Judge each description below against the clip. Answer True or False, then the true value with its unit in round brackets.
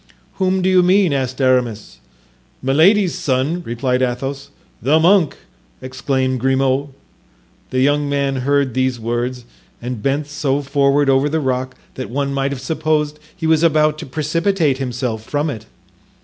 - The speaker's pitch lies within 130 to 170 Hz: True (140 Hz)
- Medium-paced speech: True (150 wpm)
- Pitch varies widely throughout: False (2.9 semitones)